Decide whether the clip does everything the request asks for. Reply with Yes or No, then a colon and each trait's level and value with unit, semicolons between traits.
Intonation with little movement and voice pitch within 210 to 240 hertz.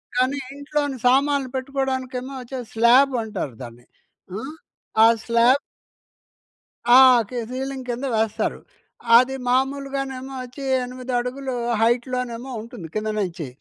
No: narrow, 2.2 semitones; very high, 255 Hz